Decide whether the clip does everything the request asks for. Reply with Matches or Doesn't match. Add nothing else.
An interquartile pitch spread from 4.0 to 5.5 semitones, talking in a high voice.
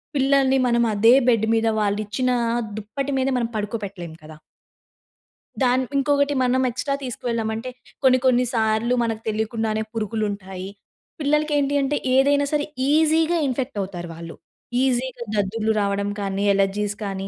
Matches